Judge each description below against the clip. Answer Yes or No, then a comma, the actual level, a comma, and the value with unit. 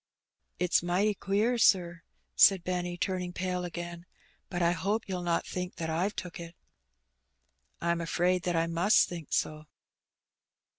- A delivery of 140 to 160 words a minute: Yes, average, 155 wpm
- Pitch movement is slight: Yes, narrow, 1.6 semitones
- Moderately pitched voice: Yes, medium, 175 Hz